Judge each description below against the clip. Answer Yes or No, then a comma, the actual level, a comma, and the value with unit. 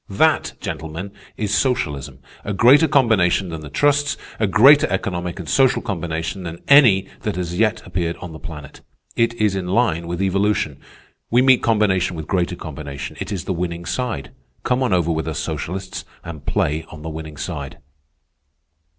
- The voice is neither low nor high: No, very low, 90 Hz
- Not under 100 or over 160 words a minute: No, average, 175 wpm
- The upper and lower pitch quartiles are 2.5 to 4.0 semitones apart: No, average, 5.3 semitones